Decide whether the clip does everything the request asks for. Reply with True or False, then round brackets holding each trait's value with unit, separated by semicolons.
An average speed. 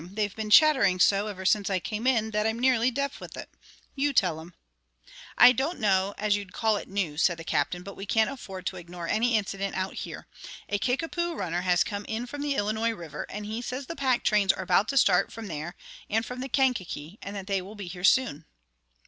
False (225 wpm)